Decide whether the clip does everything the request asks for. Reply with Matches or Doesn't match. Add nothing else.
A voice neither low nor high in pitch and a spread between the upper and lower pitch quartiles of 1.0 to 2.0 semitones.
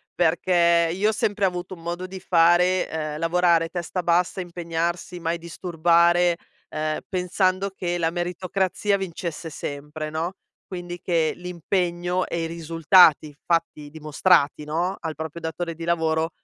Matches